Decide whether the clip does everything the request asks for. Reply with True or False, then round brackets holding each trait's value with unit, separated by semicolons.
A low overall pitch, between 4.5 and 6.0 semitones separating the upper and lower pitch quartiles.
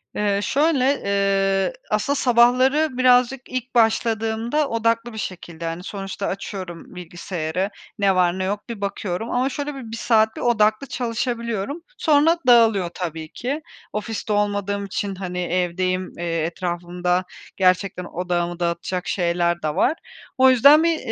False (205 Hz; 5.0 semitones)